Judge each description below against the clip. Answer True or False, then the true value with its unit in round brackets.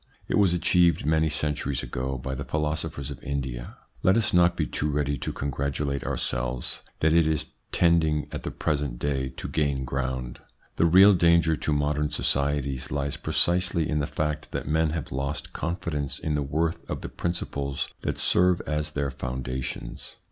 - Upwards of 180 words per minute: False (170 wpm)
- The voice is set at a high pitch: False (75 Hz)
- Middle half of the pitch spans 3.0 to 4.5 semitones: False (2.6 semitones)